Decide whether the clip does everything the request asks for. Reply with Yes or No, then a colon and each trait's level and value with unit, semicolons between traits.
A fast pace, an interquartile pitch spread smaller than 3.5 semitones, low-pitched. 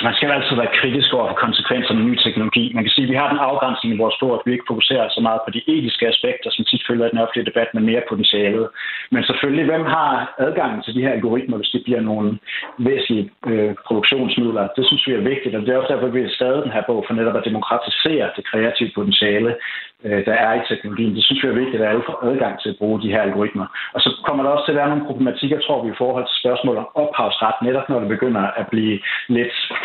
Yes: fast, 255 wpm; average, 3.1 semitones; low, 120 Hz